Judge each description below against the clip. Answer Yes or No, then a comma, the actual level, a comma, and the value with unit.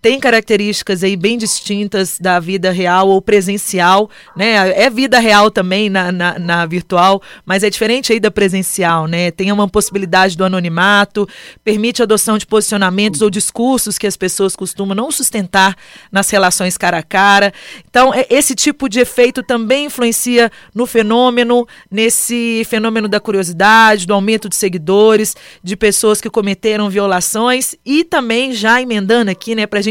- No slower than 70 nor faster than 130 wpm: No, average, 160 wpm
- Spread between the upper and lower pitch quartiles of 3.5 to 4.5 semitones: No, average, 3.1 semitones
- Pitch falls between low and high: No, high, 210 Hz